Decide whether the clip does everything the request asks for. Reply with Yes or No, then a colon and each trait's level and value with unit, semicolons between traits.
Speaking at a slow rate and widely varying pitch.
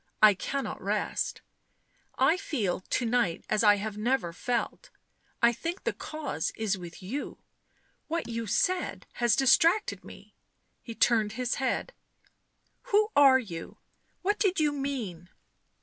No: average, 150 wpm; wide, 5.8 semitones